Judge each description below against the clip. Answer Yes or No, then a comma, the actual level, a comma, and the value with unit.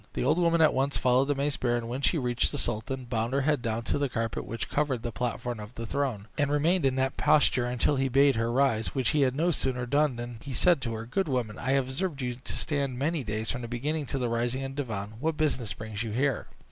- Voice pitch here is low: Yes, low, 130 Hz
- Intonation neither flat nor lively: Yes, average, 3.3 semitones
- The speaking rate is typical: No, fast, 265 wpm